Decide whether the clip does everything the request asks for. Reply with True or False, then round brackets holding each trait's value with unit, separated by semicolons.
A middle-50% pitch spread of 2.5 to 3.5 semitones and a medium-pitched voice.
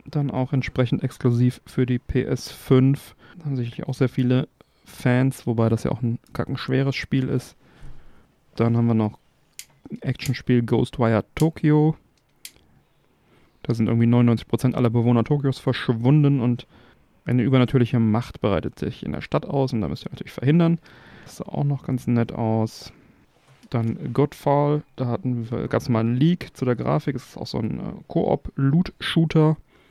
False (2.9 semitones; 125 Hz)